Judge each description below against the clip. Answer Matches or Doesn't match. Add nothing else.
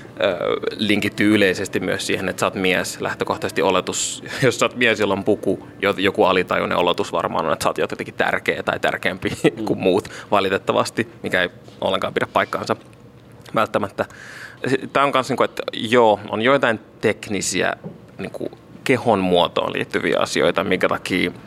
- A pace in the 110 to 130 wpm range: Doesn't match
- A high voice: Doesn't match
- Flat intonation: Matches